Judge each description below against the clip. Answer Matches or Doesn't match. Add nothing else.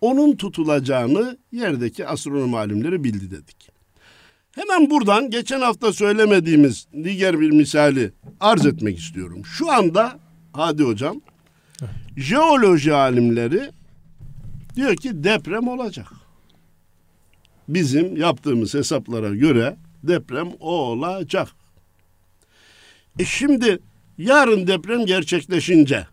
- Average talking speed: Doesn't match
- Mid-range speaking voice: Matches